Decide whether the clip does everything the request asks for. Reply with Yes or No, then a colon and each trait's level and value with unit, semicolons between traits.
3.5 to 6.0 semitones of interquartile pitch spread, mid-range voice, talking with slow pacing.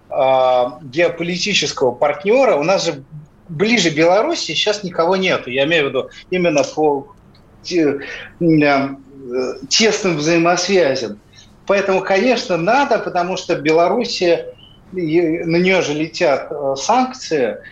Yes: average, 4.5 semitones; medium, 170 Hz; slow, 100 wpm